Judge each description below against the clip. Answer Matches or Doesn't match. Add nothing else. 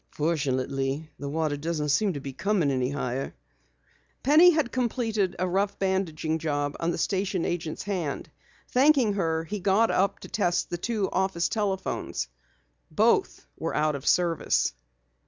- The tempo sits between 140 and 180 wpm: Matches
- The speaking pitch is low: Doesn't match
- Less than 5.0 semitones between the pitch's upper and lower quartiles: Doesn't match